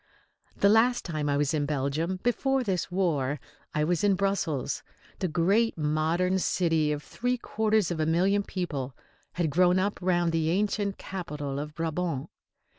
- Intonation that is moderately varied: Yes, average, 4.4 semitones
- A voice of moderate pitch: Yes, medium, 175 Hz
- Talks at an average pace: Yes, average, 160 wpm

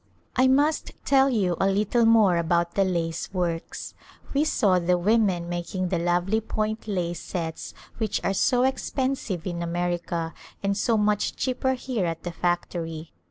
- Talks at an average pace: Yes, average, 160 wpm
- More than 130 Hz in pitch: Yes, medium, 185 Hz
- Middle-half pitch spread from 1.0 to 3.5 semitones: No, average, 4.5 semitones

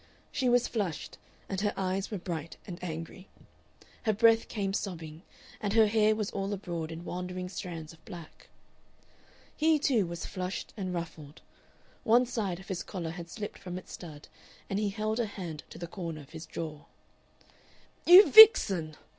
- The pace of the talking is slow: No, average, 170 wpm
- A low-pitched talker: No, medium, 185 Hz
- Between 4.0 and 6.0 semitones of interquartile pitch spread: Yes, average, 4.3 semitones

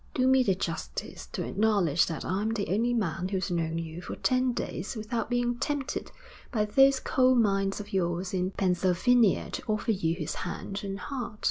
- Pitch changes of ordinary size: Yes, average, 5.0 semitones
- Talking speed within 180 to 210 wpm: Yes, average, 185 wpm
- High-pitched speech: Yes, high, 200 Hz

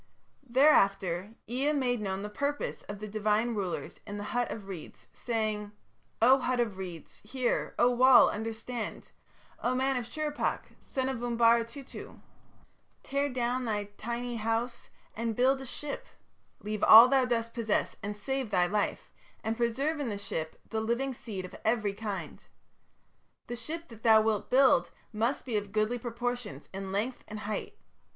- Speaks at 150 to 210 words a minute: Yes, average, 160 wpm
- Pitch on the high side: Yes, high, 230 Hz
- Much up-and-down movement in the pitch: No, average, 3.2 semitones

